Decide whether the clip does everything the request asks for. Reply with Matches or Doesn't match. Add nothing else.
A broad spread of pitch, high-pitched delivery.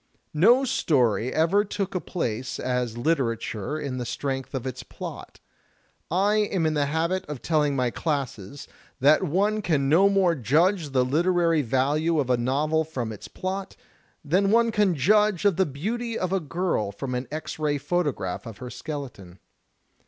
Doesn't match